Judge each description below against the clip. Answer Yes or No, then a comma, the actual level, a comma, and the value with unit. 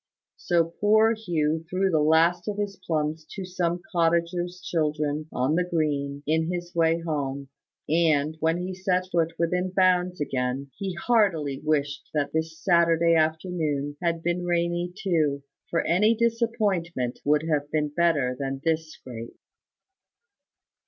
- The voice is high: No, medium, 165 Hz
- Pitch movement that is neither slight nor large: Yes, average, 3.0 semitones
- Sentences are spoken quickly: No, average, 140 wpm